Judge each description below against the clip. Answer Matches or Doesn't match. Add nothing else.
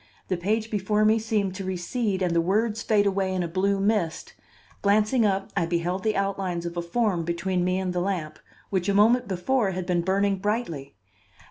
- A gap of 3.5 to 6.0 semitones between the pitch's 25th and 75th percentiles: Doesn't match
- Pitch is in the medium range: Doesn't match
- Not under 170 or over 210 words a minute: Matches